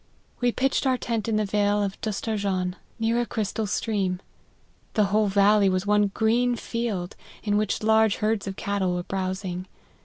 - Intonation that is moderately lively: No, narrow, 2.3 semitones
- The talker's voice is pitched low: No, high, 210 Hz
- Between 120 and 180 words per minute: Yes, average, 165 wpm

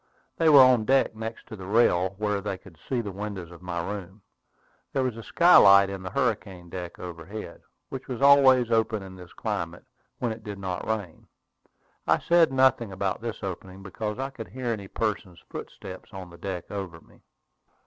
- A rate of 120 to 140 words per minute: No, average, 190 wpm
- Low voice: Yes, low, 100 Hz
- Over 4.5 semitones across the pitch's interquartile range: No, average, 4.2 semitones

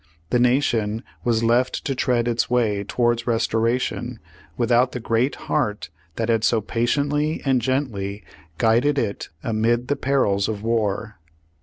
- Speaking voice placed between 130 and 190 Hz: No, low, 120 Hz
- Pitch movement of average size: No, narrow, 2.3 semitones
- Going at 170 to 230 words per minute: No, average, 140 wpm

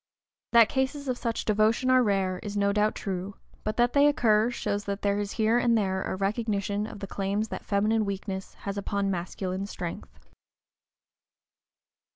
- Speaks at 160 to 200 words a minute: Yes, average, 170 wpm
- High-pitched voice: Yes, high, 205 Hz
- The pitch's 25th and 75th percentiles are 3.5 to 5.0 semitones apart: No, narrow, 2.4 semitones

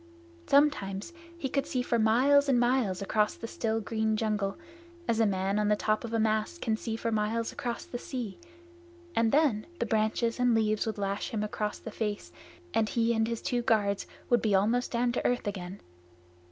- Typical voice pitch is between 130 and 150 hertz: No, high, 225 Hz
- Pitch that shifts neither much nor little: No, narrow, 2.3 semitones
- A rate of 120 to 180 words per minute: No, average, 195 wpm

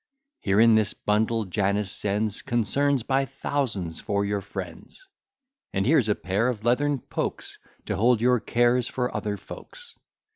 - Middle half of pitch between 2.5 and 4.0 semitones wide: Yes, average, 3.6 semitones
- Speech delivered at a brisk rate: No, average, 150 wpm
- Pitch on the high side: No, low, 110 Hz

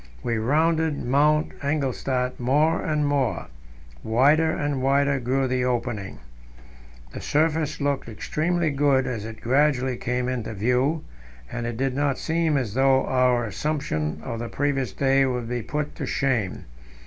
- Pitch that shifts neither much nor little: Yes, average, 3.1 semitones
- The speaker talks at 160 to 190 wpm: No, average, 150 wpm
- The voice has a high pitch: No, low, 135 Hz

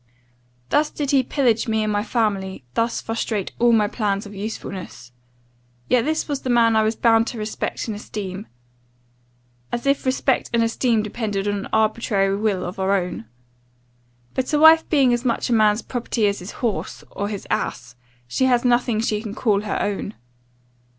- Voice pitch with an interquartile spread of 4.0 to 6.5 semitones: No, average, 2.9 semitones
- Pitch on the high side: Yes, high, 220 Hz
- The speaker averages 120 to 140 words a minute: No, average, 180 wpm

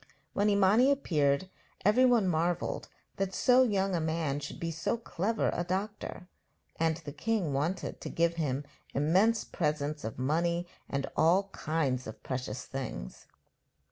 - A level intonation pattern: No, average, 5.2 semitones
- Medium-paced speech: Yes, average, 145 wpm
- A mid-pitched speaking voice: Yes, medium, 170 Hz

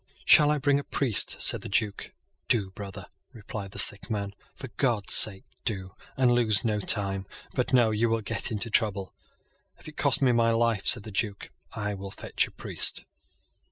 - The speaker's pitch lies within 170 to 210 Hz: No, low, 110 Hz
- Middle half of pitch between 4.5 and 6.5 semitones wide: No, average, 3.3 semitones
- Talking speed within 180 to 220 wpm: Yes, average, 190 wpm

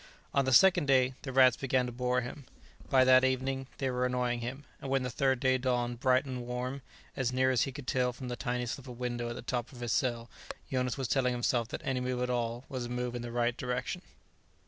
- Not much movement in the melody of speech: Yes, narrow, 1.3 semitones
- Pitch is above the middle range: No, low, 125 Hz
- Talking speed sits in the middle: No, fast, 245 wpm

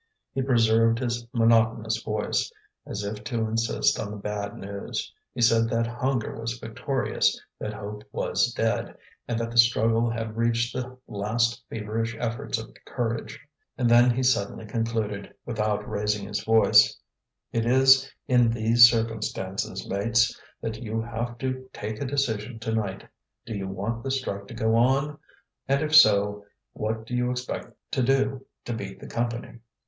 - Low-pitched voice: Yes, low, 115 Hz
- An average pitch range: No, narrow, 2.0 semitones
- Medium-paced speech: Yes, average, 160 wpm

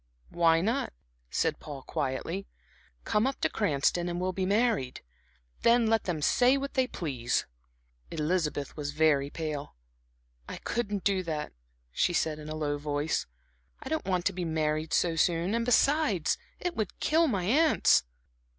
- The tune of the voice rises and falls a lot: Yes, wide, 6.7 semitones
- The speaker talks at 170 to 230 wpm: No, average, 160 wpm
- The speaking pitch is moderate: Yes, medium, 175 Hz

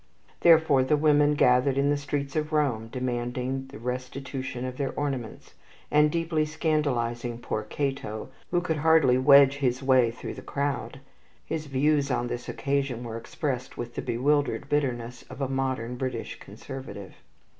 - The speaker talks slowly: No, average, 155 wpm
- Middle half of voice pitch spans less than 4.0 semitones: Yes, average, 2.9 semitones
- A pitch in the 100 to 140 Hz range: Yes, low, 135 Hz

